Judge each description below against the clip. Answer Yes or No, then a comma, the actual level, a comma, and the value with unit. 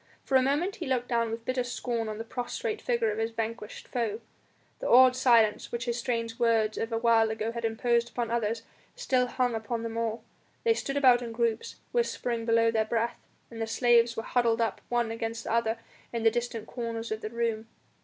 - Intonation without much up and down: Yes, narrow, 1.3 semitones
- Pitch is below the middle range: No, high, 230 Hz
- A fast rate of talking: Yes, fast, 215 wpm